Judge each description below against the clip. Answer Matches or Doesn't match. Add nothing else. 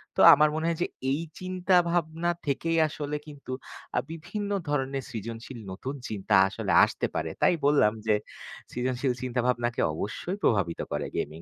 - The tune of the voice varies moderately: Doesn't match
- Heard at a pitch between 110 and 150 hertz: Matches